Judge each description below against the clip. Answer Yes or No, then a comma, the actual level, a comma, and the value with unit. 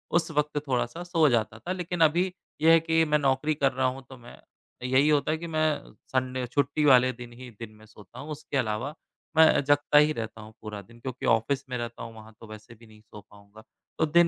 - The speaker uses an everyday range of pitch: Yes, average, 4.8 semitones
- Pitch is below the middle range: Yes, low, 130 Hz